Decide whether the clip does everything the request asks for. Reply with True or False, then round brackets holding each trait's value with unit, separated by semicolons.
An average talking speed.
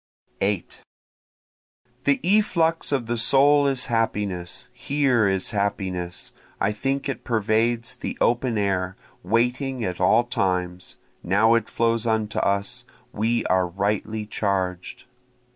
False (120 wpm)